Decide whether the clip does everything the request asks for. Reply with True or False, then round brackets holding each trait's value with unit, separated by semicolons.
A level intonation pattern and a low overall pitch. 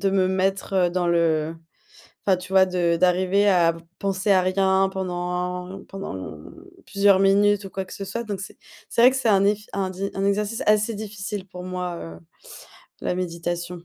False (1.8 semitones; 190 Hz)